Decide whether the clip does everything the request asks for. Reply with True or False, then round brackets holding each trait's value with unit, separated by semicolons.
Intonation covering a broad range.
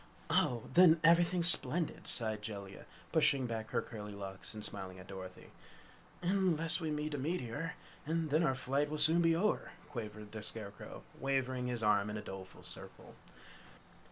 True (7.5 semitones)